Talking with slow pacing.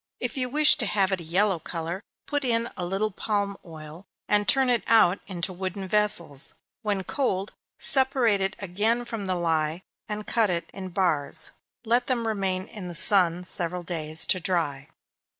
No: average, 175 wpm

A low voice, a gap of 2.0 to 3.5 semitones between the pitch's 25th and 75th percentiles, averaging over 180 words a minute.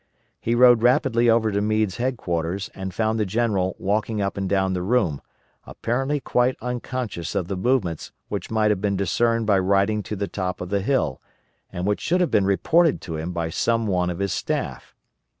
No: low, 105 Hz; average, 3.9 semitones; average, 195 wpm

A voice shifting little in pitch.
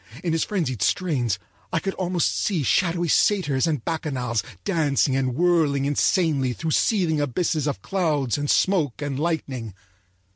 No: average, 4.4 semitones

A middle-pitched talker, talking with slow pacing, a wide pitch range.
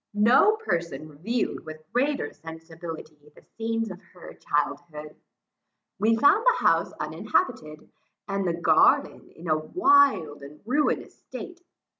Yes: medium, 175 Hz; slow, 125 wpm; wide, 7.6 semitones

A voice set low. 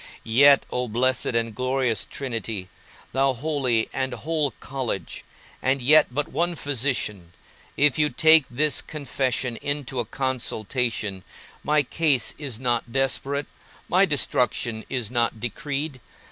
Yes: low, 130 Hz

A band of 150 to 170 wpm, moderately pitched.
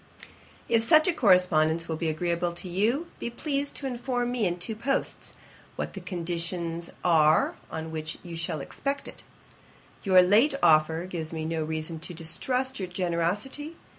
Yes: average, 165 wpm; medium, 175 Hz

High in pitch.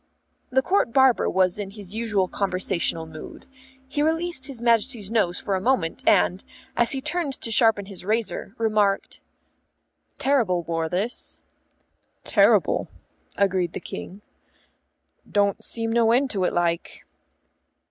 Yes: high, 210 Hz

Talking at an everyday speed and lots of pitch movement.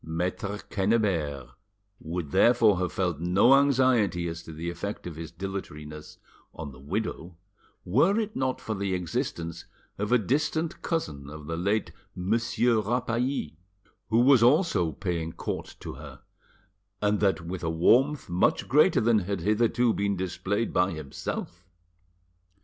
Yes: average, 145 wpm; wide, 6.0 semitones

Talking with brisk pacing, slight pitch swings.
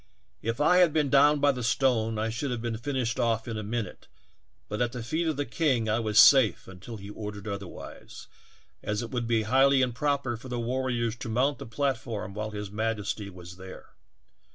No: fast, 210 wpm; average, 3.6 semitones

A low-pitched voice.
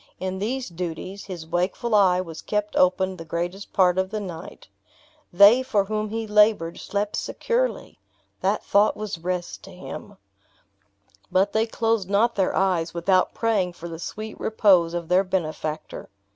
No: high, 190 Hz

